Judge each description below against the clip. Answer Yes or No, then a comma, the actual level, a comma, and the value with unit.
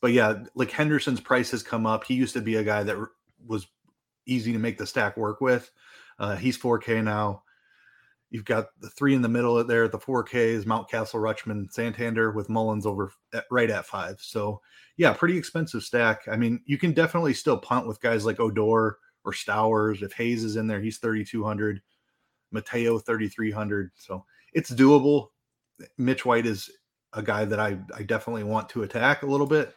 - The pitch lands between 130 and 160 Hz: No, low, 115 Hz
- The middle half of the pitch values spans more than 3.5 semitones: No, narrow, 2.6 semitones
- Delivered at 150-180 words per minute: No, average, 190 wpm